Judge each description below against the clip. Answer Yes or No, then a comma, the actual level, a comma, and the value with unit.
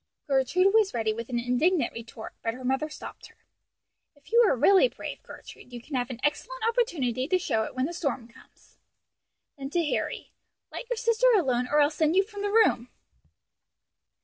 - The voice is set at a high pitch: Yes, very high, 290 Hz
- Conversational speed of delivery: Yes, average, 190 wpm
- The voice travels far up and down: Yes, wide, 7.8 semitones